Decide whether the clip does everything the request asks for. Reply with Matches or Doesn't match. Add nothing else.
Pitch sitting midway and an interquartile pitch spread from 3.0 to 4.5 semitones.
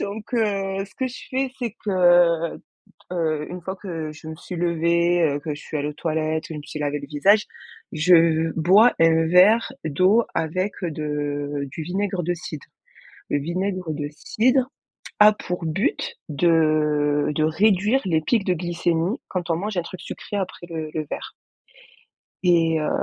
Matches